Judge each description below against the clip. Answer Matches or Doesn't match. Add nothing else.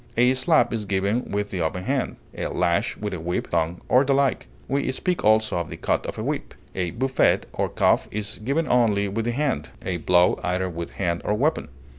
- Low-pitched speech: Matches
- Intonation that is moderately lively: Doesn't match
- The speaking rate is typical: Doesn't match